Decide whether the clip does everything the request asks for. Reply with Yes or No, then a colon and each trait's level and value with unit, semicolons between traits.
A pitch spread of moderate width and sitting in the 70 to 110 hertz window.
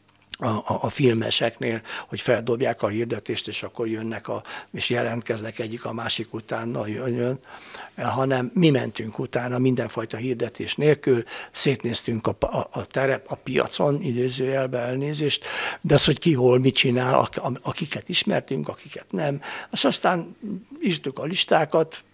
No: average, 3.5 semitones; low, 125 Hz